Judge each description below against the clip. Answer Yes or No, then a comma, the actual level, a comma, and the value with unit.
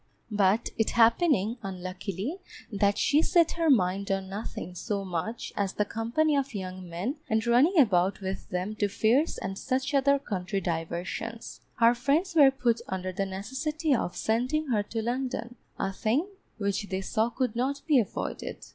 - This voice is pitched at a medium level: No, high, 220 Hz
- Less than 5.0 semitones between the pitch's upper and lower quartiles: No, wide, 5.6 semitones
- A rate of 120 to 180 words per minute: Yes, average, 165 wpm